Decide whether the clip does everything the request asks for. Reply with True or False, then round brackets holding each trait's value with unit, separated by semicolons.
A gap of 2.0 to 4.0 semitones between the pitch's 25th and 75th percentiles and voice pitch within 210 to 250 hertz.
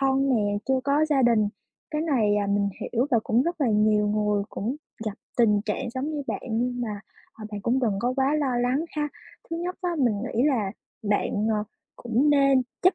False (4.6 semitones; 245 Hz)